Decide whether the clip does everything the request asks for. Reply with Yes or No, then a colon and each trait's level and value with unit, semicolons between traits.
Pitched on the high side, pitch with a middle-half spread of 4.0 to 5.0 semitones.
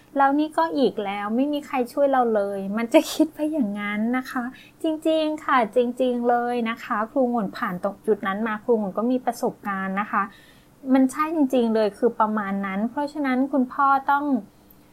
Yes: high, 245 Hz; average, 4.5 semitones